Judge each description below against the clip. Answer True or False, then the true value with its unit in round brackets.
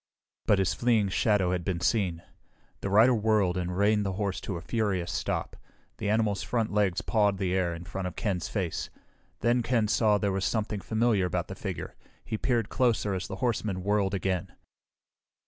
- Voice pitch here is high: False (100 Hz)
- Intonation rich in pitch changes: False (2.9 semitones)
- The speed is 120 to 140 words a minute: False (185 wpm)